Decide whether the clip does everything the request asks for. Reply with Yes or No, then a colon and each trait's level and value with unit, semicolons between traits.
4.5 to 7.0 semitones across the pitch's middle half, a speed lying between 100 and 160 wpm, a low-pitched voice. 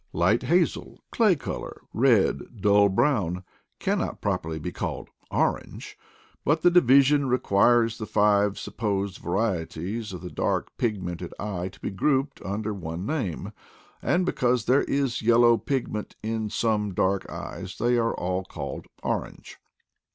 Yes: average, 4.8 semitones; average, 140 wpm; low, 110 Hz